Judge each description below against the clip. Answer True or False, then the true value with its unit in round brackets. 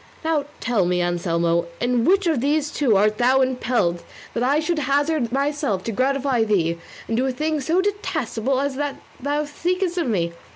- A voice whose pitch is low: False (265 Hz)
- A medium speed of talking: True (180 wpm)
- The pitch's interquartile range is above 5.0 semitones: True (5.5 semitones)